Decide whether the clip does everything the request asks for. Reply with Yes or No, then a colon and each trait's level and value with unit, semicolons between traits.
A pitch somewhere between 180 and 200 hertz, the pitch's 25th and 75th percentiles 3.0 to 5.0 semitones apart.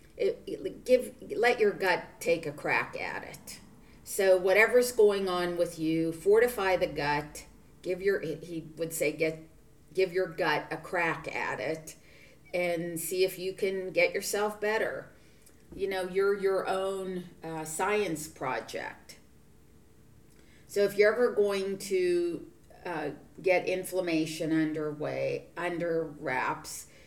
Yes: medium, 185 Hz; average, 4.1 semitones